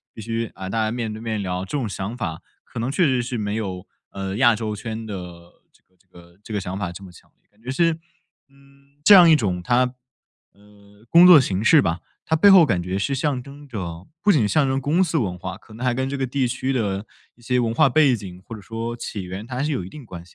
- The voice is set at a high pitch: No, low, 115 Hz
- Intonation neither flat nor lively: No, wide, 5.8 semitones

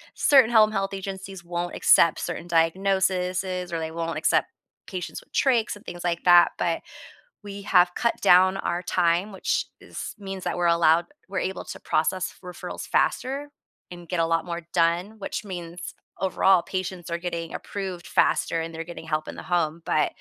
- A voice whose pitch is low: No, medium, 180 Hz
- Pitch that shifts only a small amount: Yes, narrow, 2.3 semitones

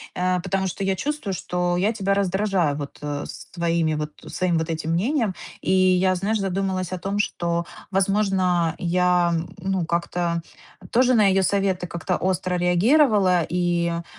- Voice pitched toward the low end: No, medium, 185 Hz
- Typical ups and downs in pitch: No, narrow, 2.2 semitones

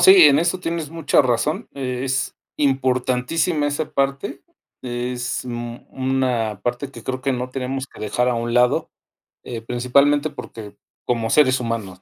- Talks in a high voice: No, low, 130 Hz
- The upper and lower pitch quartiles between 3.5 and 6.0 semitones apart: No, narrow, 2.6 semitones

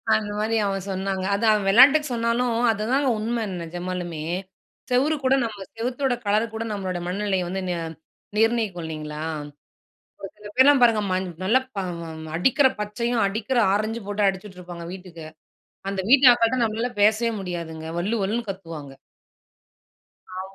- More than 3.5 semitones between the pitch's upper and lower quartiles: Yes, average, 3.9 semitones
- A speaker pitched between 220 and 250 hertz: No, high, 210 Hz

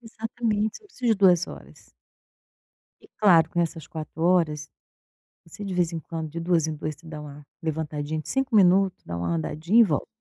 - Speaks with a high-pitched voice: No, medium, 165 Hz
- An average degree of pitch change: Yes, average, 4.3 semitones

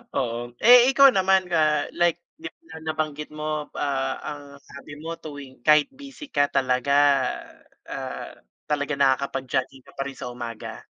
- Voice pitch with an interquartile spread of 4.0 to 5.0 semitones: No, average, 3.6 semitones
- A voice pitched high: No, medium, 145 Hz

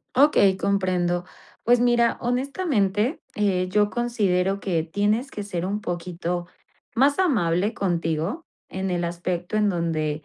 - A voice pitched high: Yes, high, 195 Hz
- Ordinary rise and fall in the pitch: Yes, average, 4.8 semitones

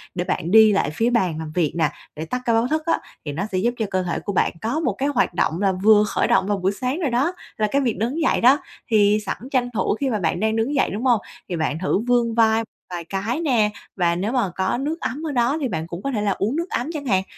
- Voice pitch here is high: Yes, high, 220 Hz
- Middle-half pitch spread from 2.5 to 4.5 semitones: No, average, 5.1 semitones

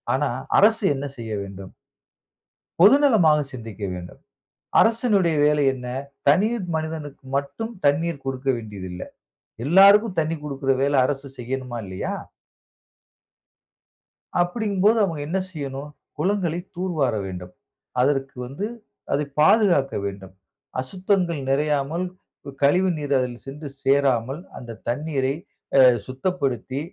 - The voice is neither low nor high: Yes, medium, 145 Hz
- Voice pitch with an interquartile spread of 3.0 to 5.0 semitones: No, wide, 5.4 semitones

